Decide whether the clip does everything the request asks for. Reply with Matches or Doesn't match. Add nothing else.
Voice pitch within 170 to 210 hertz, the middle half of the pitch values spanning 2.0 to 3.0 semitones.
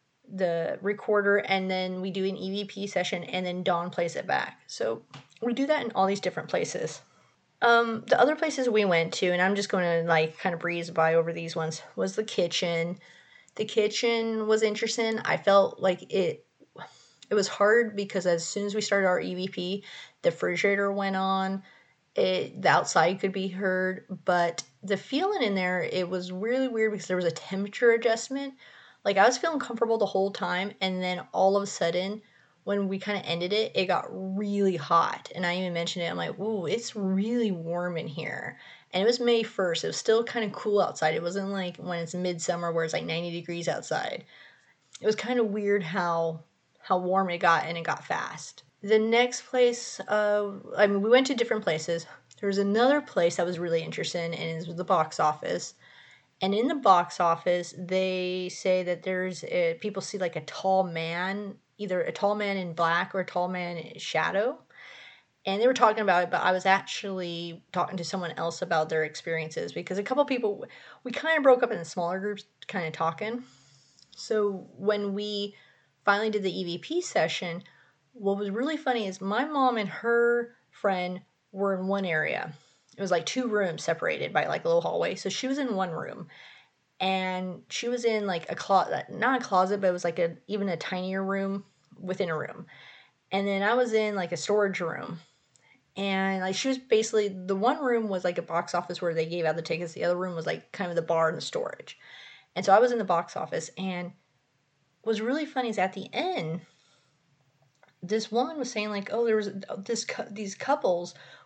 Doesn't match